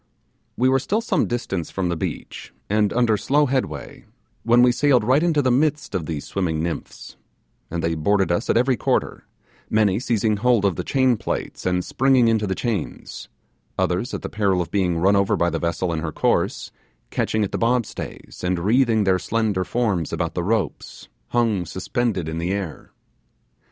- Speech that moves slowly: No, average, 185 wpm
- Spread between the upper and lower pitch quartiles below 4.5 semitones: No, wide, 5.4 semitones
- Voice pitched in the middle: No, low, 105 Hz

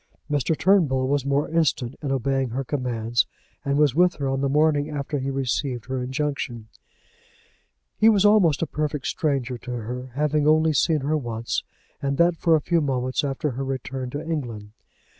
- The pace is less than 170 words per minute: No, average, 180 wpm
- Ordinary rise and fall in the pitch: Yes, average, 3.0 semitones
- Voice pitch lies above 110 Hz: Yes, medium, 140 Hz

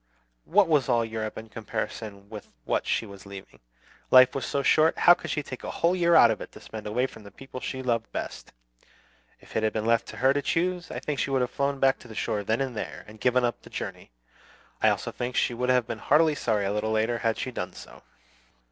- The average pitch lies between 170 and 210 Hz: No, low, 120 Hz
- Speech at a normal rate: No, fast, 245 wpm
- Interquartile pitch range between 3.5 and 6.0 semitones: Yes, average, 3.8 semitones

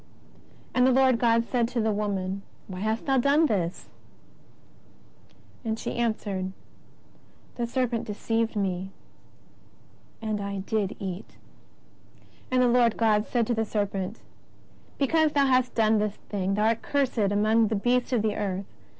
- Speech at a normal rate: Yes, average, 150 wpm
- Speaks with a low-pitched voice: No, high, 220 Hz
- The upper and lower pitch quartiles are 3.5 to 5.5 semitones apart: No, average, 3.1 semitones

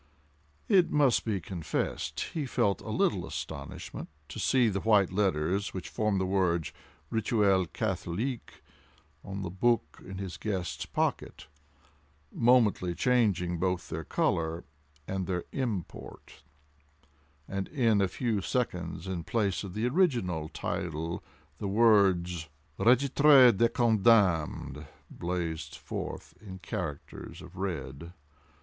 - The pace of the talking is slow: Yes, slow, 120 wpm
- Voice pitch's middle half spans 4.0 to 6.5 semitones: Yes, average, 4.7 semitones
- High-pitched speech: No, very low, 95 Hz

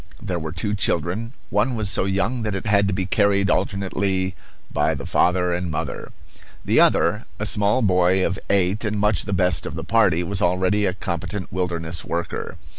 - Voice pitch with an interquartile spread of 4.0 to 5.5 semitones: No, narrow, 2.4 semitones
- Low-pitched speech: Yes, very low, 95 Hz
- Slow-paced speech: No, average, 190 wpm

